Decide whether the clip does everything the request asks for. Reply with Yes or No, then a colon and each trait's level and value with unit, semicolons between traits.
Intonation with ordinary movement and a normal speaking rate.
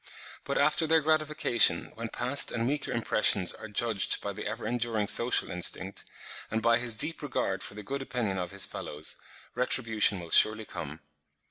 Yes: average, 3.8 semitones; average, 170 wpm